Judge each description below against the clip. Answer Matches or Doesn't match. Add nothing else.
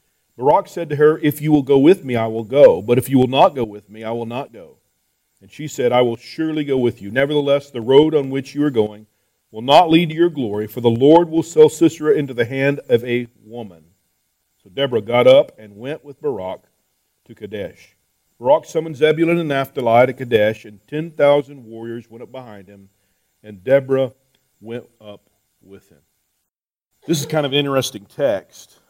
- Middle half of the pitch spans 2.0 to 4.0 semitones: Doesn't match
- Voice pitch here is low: Matches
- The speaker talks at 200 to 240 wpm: Matches